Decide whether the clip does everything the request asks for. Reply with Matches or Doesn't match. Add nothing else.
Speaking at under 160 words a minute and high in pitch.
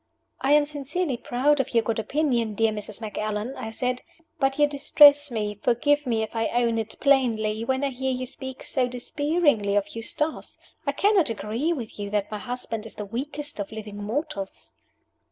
Doesn't match